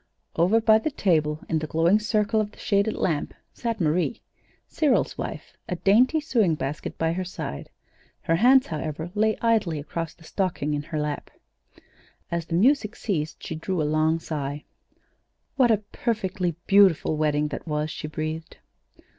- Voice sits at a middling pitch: Yes, medium, 170 Hz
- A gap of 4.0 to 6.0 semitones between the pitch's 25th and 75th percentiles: Yes, wide, 5.5 semitones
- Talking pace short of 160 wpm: No, average, 165 wpm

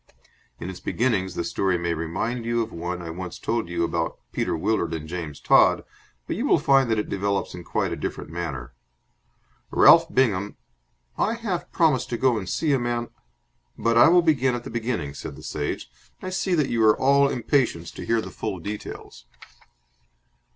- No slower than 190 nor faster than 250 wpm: Yes, average, 195 wpm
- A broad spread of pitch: Yes, wide, 6.9 semitones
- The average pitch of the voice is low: Yes, low, 110 Hz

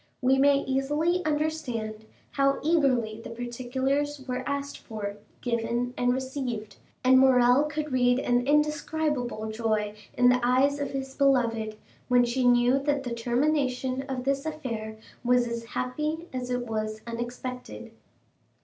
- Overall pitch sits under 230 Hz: No, very high, 250 Hz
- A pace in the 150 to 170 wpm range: No, average, 140 wpm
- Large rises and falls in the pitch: No, average, 2.7 semitones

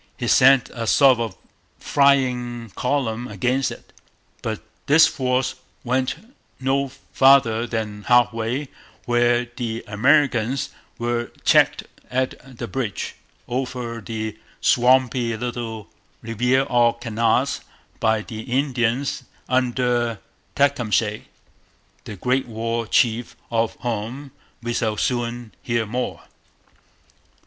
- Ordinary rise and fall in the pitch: No, narrow, 2.2 semitones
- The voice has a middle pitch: No, low, 120 Hz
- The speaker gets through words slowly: Yes, slow, 105 wpm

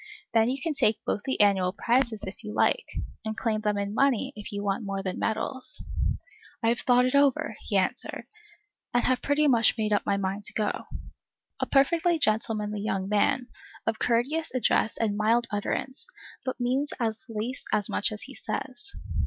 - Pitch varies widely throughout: No, average, 3.9 semitones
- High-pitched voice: Yes, high, 225 Hz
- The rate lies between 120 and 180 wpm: No, average, 190 wpm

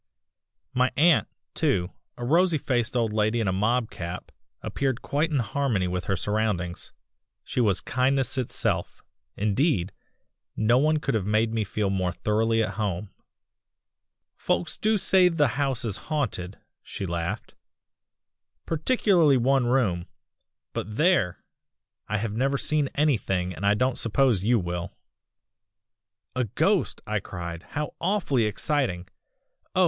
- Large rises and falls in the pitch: Yes, wide, 6.1 semitones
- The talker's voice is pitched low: Yes, low, 115 Hz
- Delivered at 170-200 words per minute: No, slow, 135 wpm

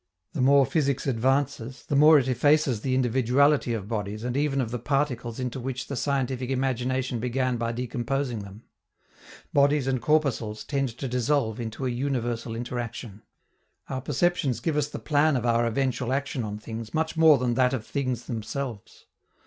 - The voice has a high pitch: No, low, 130 Hz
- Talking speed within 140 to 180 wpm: Yes, average, 170 wpm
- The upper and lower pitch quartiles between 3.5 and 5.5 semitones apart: No, average, 2.9 semitones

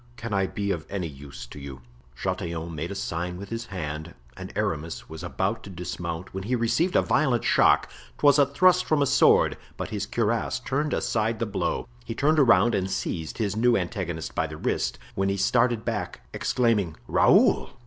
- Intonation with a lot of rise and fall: Yes, wide, 5.9 semitones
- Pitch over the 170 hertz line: No, low, 100 Hz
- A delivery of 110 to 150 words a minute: No, average, 190 wpm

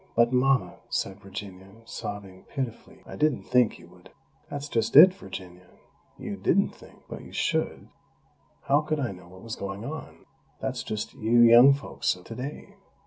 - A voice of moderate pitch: No, low, 115 Hz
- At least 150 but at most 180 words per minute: Yes, average, 170 wpm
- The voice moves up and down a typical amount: No, wide, 5.8 semitones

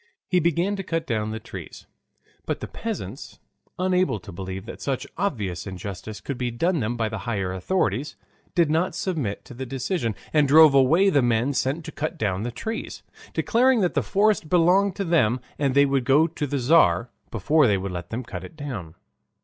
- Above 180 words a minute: Yes, average, 200 wpm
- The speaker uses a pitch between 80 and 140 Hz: Yes, low, 135 Hz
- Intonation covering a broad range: Yes, wide, 7.5 semitones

